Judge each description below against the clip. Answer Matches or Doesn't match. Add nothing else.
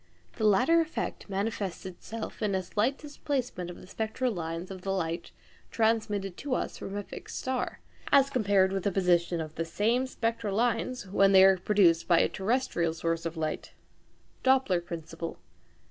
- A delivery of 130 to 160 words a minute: Doesn't match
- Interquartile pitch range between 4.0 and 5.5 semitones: Matches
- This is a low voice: Doesn't match